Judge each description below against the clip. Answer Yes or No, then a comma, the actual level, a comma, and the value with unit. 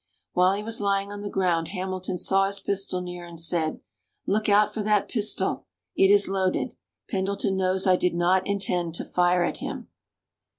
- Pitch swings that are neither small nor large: No, narrow, 1.9 semitones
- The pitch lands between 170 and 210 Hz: Yes, high, 190 Hz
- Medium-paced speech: Yes, average, 180 wpm